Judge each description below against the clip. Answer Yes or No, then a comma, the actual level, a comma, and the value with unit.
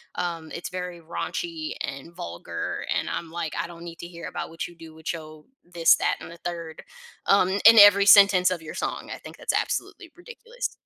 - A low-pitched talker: No, medium, 170 Hz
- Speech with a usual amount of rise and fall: Yes, average, 3.3 semitones